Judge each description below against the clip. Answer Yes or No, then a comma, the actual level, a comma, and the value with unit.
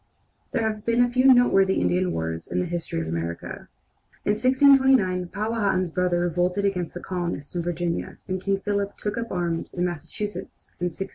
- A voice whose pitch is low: No, medium, 185 Hz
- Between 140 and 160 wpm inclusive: No, average, 180 wpm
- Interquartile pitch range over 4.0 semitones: No, average, 3.7 semitones